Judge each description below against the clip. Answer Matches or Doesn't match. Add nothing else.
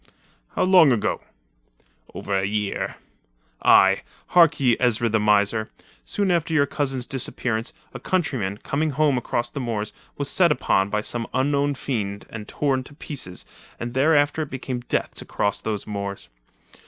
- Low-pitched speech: Matches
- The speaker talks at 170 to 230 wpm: Doesn't match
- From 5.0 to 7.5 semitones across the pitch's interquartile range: Matches